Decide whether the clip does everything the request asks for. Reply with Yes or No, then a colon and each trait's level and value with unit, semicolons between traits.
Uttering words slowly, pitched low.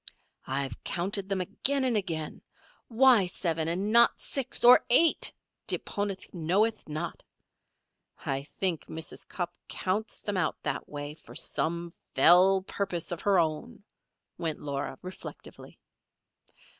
No: slow, 130 wpm; medium, 185 Hz